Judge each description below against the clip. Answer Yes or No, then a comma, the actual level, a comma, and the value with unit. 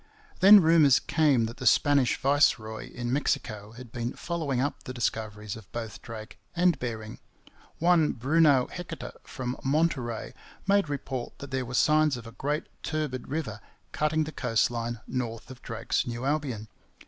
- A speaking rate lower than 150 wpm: No, average, 160 wpm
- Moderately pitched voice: No, low, 130 Hz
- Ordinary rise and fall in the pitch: Yes, average, 4.7 semitones